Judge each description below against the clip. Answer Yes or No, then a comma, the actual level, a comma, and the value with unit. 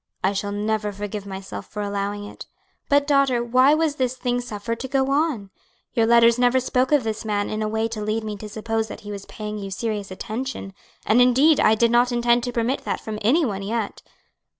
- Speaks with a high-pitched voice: Yes, high, 225 Hz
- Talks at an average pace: No, fast, 220 wpm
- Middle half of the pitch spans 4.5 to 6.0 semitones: No, average, 3.2 semitones